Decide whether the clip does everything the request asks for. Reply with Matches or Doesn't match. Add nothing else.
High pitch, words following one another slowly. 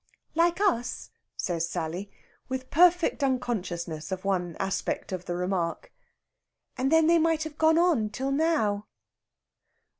Matches